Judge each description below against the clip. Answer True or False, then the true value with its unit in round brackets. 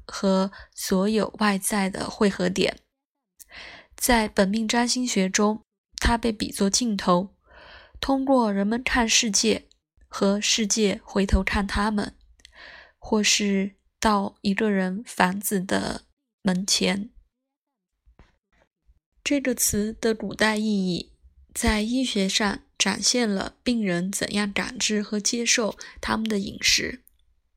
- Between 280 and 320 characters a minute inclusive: False (170 characters per minute)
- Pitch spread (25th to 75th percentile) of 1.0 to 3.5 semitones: True (2.7 semitones)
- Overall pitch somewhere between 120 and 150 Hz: False (210 Hz)